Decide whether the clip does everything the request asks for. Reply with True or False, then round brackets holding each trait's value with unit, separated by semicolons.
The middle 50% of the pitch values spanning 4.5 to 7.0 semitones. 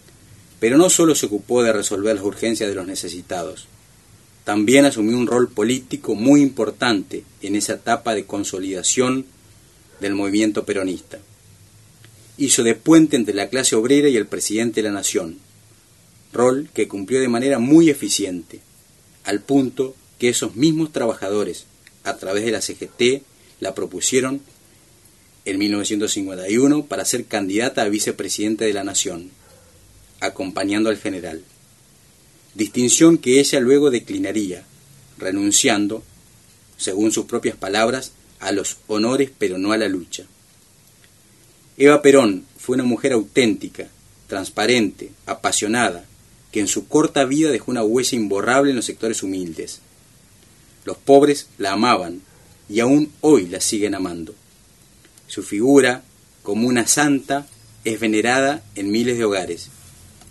True (5.0 semitones)